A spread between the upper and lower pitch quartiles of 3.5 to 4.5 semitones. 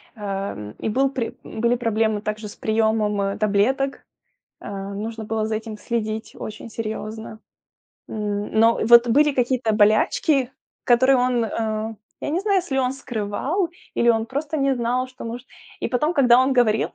No: average, 3.1 semitones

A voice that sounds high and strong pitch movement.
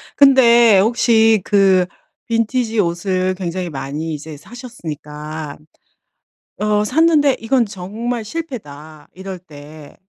Yes: high, 195 Hz; wide, 6.8 semitones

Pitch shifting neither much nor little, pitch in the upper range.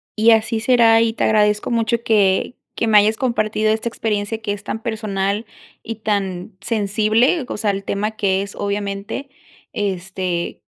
No: narrow, 2.0 semitones; high, 215 Hz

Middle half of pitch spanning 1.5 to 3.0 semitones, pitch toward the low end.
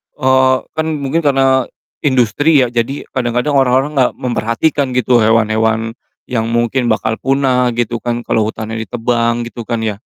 Yes: narrow, 2.5 semitones; low, 120 Hz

